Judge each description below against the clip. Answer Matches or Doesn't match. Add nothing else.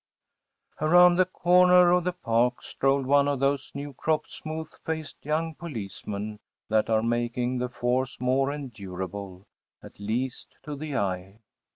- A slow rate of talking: Doesn't match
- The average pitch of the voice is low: Matches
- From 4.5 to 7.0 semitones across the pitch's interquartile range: Matches